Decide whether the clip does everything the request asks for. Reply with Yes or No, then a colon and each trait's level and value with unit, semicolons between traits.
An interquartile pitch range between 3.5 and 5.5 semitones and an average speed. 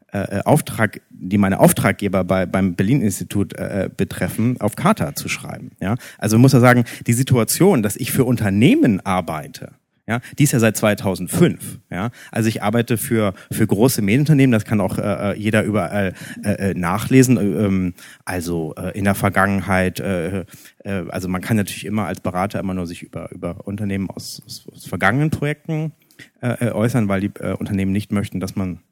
Yes: average, 3.9 semitones; average, 180 wpm